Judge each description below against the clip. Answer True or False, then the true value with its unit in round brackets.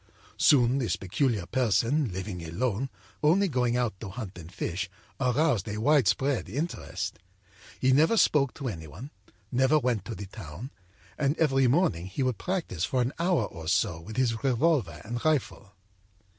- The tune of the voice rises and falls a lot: True (6.2 semitones)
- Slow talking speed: False (160 wpm)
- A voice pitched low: True (120 Hz)